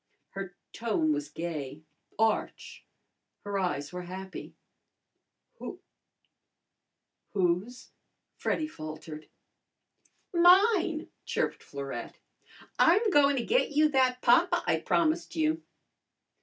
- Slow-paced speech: Yes, slow, 95 wpm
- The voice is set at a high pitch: Yes, high, 225 Hz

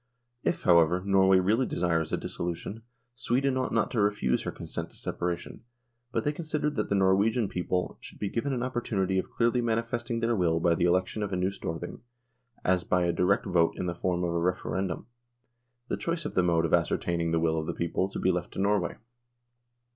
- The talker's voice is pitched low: Yes, very low, 95 Hz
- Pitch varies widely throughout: No, average, 4.8 semitones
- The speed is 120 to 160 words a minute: No, fast, 205 wpm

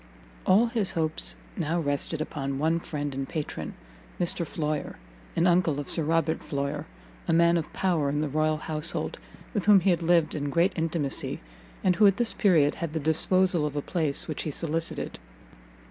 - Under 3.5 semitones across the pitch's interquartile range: Yes, average, 2.7 semitones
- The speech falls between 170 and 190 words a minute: Yes, average, 180 wpm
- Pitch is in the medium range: Yes, medium, 160 Hz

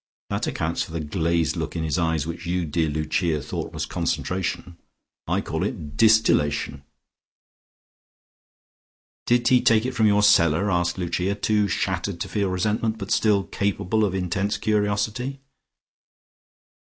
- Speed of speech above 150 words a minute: No, average, 140 wpm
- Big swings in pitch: No, average, 4.0 semitones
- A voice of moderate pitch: No, very low, 95 Hz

